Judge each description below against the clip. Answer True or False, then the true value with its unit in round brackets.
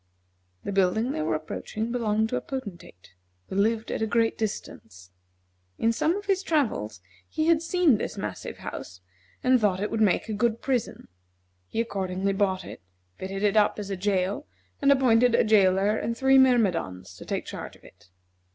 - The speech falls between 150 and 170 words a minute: False (180 wpm)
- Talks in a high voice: True (215 Hz)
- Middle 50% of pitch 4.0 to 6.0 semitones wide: True (4.6 semitones)